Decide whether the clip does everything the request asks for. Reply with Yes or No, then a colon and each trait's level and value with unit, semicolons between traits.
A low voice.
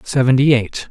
Yes: low, 130 Hz